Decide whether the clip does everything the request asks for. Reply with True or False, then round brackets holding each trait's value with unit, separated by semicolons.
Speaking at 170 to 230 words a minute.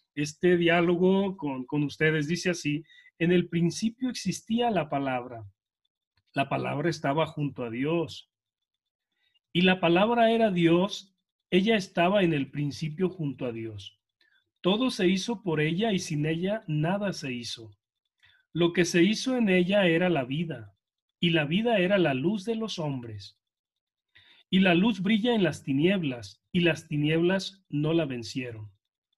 False (150 wpm)